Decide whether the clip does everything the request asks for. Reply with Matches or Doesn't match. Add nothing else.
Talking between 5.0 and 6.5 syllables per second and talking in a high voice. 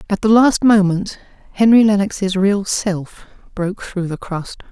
Doesn't match